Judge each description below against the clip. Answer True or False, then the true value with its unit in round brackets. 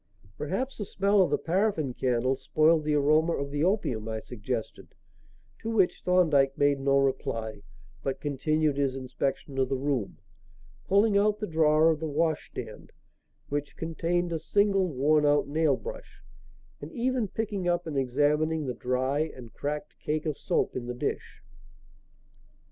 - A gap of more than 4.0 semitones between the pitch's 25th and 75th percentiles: True (4.5 semitones)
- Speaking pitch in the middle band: True (150 Hz)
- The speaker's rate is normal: True (155 wpm)